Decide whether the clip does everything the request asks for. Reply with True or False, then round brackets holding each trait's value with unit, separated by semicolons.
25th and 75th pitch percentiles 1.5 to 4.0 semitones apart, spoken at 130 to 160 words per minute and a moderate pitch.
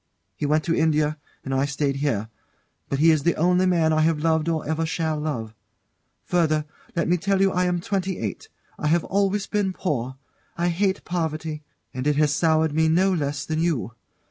False (2.9 semitones; 195 wpm; 160 Hz)